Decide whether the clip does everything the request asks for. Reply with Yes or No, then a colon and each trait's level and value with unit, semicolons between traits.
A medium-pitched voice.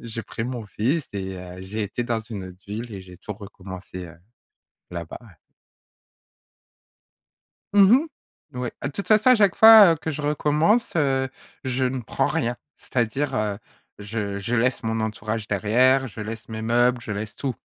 No: low, 115 Hz